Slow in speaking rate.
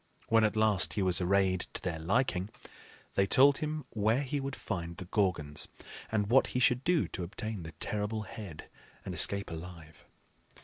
No: average, 175 wpm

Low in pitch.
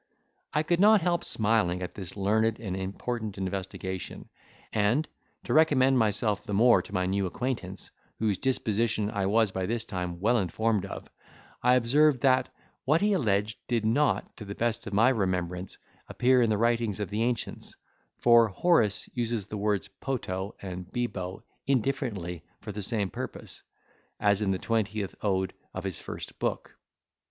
Yes: low, 110 Hz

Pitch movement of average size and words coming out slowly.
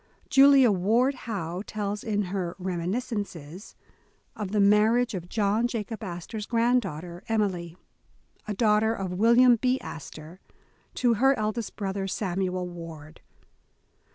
Yes: average, 4.2 semitones; slow, 130 wpm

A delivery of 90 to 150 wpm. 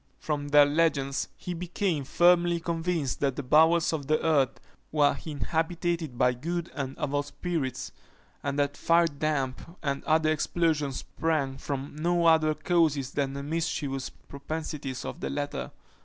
Yes: average, 140 wpm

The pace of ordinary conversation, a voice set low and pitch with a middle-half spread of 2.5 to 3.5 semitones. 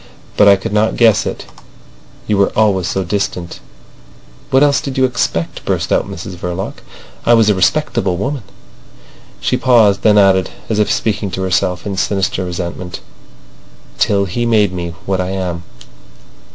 Yes: average, 165 wpm; very low, 95 Hz; average, 3.0 semitones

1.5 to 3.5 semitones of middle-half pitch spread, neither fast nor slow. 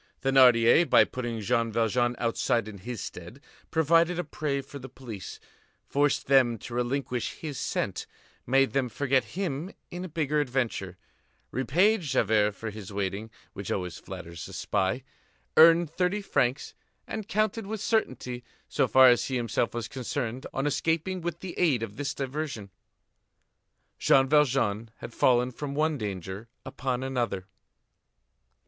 No: average, 4.7 semitones; average, 145 wpm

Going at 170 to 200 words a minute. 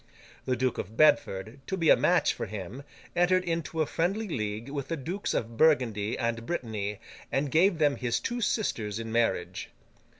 Yes: average, 175 wpm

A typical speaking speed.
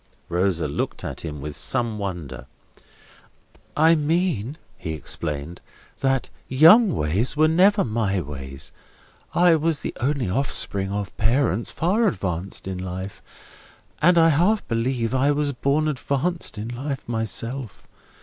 No: slow, 130 wpm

